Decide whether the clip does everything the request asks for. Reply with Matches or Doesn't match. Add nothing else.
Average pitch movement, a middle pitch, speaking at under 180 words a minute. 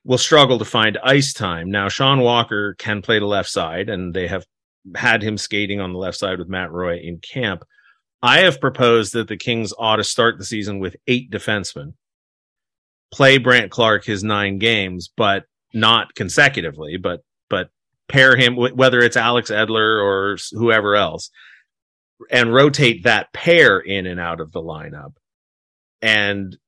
Doesn't match